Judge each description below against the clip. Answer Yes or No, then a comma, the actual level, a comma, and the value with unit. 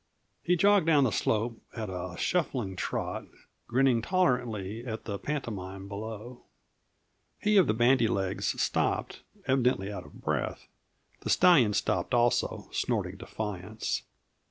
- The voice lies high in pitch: No, low, 115 Hz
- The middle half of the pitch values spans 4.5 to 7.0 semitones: Yes, average, 4.8 semitones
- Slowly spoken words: Yes, slow, 130 wpm